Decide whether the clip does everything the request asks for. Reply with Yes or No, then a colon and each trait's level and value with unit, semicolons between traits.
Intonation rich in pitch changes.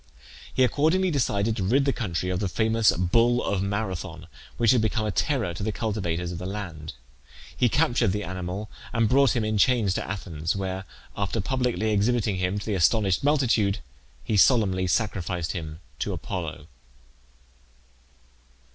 No: average, 4.1 semitones